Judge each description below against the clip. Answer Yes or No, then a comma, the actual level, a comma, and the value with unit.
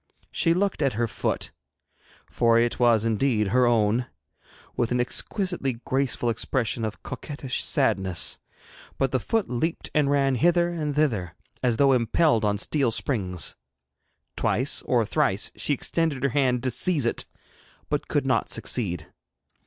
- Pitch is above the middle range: No, low, 125 Hz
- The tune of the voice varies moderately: Yes, average, 4.0 semitones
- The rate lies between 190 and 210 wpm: No, average, 145 wpm